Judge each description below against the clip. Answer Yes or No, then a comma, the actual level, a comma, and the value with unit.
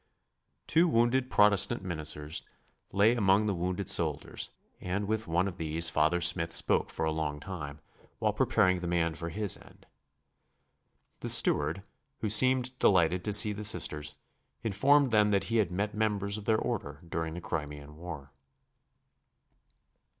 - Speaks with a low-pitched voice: Yes, very low, 95 Hz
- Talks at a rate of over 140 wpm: Yes, average, 150 wpm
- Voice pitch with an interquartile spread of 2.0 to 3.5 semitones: No, average, 4.8 semitones